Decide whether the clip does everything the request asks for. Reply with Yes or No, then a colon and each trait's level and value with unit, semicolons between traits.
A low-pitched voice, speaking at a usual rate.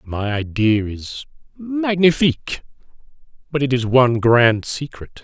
No: low, 130 Hz; slow, 115 wpm